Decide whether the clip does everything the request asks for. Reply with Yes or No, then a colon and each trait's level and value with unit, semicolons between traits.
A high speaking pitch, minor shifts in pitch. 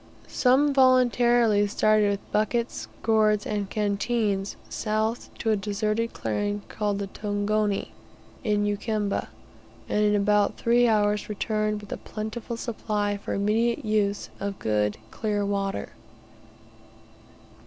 Yes: high, 210 Hz; narrow, 1.5 semitones